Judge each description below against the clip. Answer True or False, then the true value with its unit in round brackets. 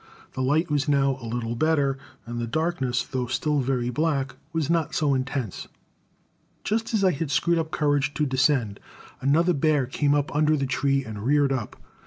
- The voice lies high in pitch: False (140 Hz)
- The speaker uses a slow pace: False (185 wpm)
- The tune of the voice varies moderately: True (3.0 semitones)